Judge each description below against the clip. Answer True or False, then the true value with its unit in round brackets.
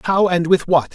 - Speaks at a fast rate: True (255 wpm)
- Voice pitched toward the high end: False (170 Hz)